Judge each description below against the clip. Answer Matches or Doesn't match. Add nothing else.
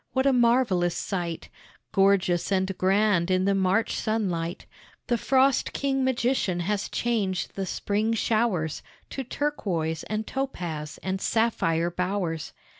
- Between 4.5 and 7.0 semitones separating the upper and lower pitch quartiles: Matches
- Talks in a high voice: Matches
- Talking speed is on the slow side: Matches